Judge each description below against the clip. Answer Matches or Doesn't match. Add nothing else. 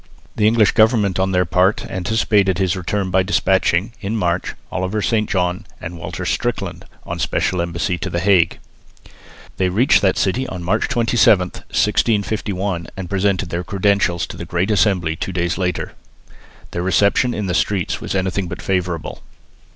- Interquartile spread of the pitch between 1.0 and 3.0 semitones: Matches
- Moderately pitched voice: Doesn't match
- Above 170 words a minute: Doesn't match